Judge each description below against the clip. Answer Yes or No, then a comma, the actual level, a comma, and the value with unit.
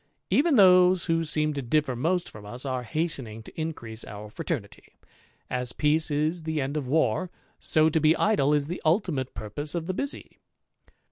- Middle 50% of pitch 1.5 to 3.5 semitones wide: No, average, 4.4 semitones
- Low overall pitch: No, medium, 155 Hz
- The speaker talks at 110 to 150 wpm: No, average, 180 wpm